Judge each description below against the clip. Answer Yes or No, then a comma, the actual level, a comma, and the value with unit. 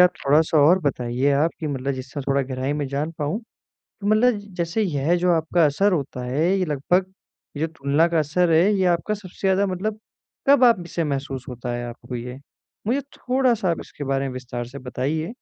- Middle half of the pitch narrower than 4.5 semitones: No, average, 4.9 semitones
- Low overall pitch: No, medium, 155 Hz